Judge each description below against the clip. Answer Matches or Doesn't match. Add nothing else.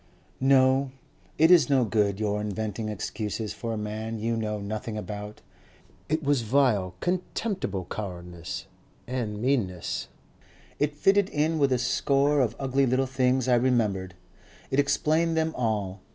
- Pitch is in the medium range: Doesn't match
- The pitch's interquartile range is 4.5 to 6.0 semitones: Matches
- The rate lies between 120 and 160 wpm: Matches